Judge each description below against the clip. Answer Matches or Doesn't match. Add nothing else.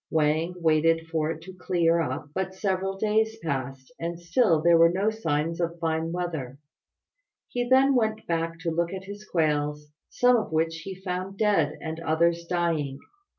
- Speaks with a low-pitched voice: Doesn't match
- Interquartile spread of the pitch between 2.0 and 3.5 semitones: Matches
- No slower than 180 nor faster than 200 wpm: Doesn't match